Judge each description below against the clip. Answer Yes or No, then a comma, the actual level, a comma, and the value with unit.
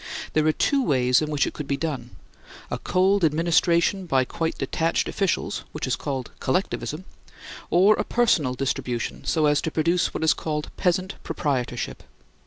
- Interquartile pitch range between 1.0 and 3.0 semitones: No, average, 4.7 semitones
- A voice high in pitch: No, medium, 155 Hz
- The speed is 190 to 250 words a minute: No, average, 165 wpm